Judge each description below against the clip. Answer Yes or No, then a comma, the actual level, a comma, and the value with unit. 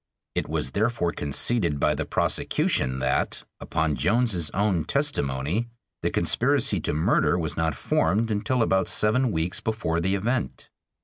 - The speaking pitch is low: Yes, very low, 90 Hz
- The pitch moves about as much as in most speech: No, wide, 6.1 semitones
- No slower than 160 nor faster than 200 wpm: No, average, 140 wpm